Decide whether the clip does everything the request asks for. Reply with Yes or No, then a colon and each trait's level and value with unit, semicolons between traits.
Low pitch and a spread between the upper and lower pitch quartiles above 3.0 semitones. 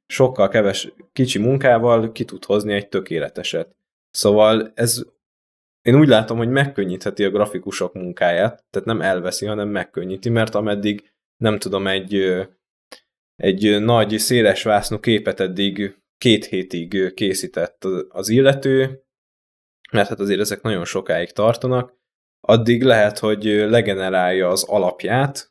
Yes: low, 105 Hz; average, 3.6 semitones